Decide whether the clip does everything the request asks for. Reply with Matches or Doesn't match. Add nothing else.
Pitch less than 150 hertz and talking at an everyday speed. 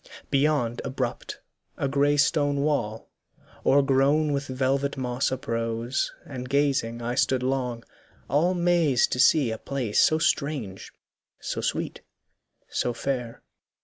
Doesn't match